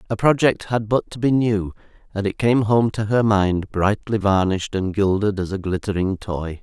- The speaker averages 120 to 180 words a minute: No, average, 200 wpm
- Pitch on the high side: No, low, 105 Hz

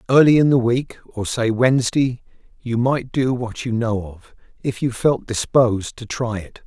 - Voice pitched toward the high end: No, low, 120 Hz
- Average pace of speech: Yes, average, 190 wpm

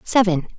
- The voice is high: Yes, high, 200 Hz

